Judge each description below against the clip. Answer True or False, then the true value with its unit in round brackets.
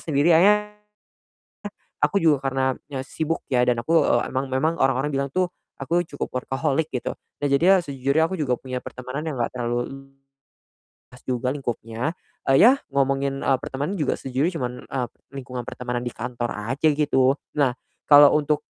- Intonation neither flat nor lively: True (3.2 semitones)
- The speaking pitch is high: False (135 Hz)